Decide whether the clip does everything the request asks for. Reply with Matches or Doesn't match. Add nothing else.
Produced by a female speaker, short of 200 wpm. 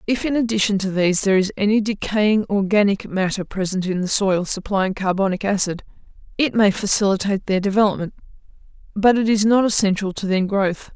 Matches